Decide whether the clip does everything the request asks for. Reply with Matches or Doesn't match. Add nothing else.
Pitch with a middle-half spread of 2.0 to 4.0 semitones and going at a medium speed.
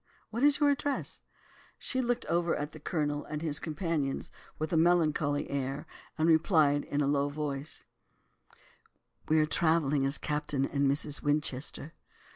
Matches